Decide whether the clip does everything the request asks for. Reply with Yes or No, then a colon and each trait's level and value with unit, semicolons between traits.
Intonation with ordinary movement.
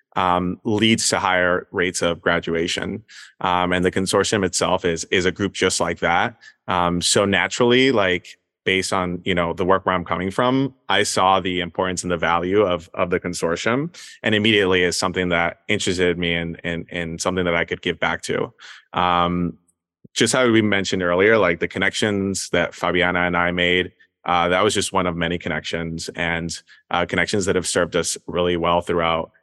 No: narrow, 1.9 semitones